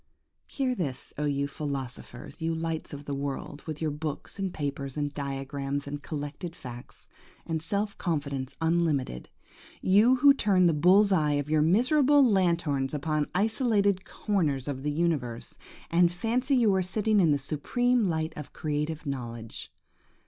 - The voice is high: No, medium, 155 Hz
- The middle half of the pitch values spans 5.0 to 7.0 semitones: Yes, average, 5.3 semitones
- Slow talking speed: No, average, 150 wpm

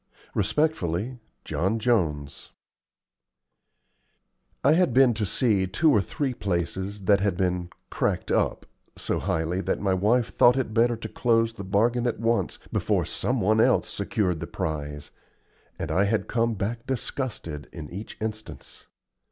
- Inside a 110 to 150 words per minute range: Yes, average, 145 wpm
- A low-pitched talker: Yes, low, 105 Hz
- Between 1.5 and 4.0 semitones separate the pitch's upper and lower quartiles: No, average, 4.4 semitones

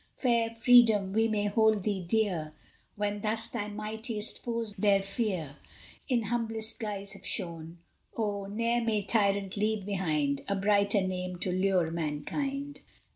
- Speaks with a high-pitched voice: Yes, high, 205 Hz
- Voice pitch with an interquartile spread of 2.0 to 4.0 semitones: Yes, average, 2.8 semitones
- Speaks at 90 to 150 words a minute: Yes, average, 140 wpm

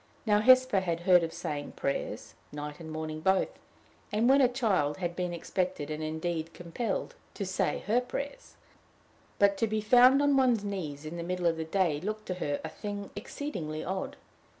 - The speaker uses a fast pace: No, average, 185 wpm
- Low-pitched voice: No, medium, 185 Hz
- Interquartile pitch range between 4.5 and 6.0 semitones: Yes, average, 5.1 semitones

